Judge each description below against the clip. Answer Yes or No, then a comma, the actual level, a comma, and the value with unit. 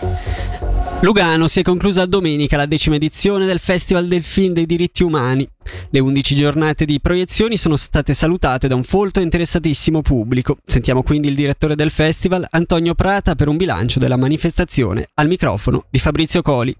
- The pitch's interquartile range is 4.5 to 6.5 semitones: Yes, average, 4.8 semitones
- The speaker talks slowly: No, fast, 170 wpm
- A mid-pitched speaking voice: Yes, medium, 155 Hz